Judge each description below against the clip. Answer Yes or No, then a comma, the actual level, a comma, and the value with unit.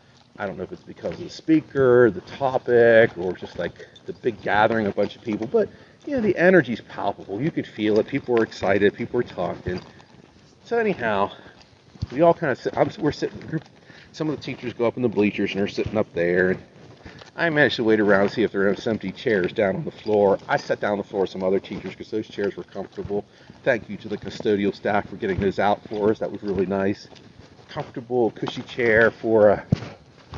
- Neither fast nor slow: No, fast, 230 wpm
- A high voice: No, low, 115 Hz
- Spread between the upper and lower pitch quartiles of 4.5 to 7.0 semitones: Yes, average, 5.2 semitones